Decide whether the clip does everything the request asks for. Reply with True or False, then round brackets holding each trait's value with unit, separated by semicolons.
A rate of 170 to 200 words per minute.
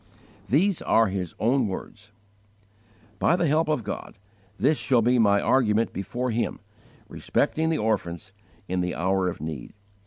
False (150 wpm)